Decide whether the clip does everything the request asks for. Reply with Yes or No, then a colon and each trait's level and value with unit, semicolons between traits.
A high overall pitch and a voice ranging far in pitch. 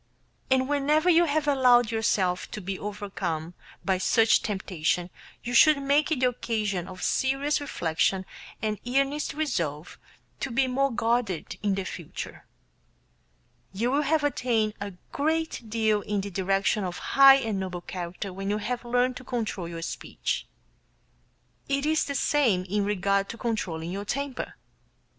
Yes: high, 220 Hz; wide, 6.1 semitones